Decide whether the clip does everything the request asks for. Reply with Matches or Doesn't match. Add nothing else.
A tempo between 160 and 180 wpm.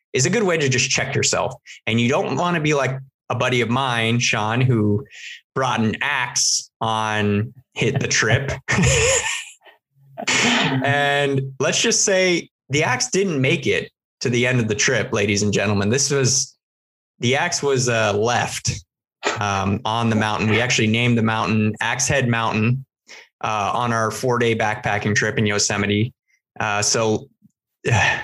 Matches